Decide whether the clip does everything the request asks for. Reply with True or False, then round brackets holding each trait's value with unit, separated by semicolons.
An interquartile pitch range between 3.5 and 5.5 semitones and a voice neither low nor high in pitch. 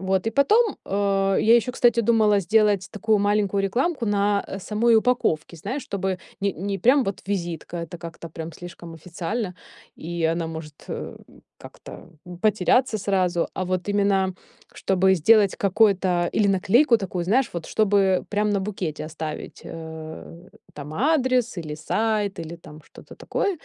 False (4.0 semitones; 195 Hz)